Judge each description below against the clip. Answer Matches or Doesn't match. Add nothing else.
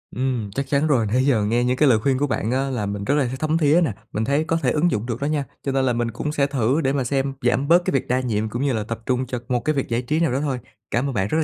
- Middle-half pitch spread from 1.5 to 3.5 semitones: Matches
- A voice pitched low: Matches